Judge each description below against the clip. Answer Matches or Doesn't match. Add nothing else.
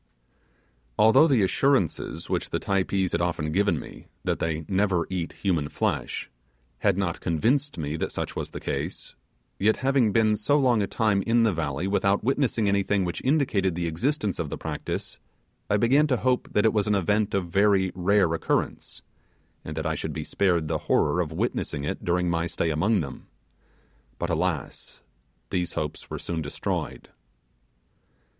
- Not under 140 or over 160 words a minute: Doesn't match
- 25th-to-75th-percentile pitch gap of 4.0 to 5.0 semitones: Matches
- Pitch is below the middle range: Matches